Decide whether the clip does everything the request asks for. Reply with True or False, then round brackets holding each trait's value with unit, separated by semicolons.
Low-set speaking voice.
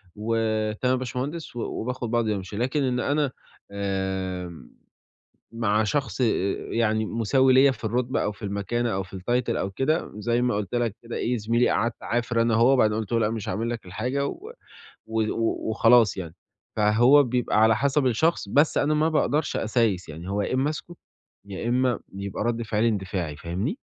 True (115 Hz)